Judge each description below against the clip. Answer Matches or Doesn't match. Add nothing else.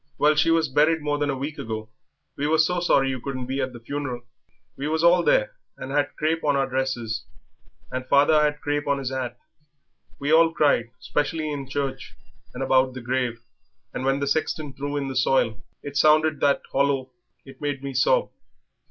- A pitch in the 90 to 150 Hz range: Matches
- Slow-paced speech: Doesn't match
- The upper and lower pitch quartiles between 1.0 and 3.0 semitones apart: Matches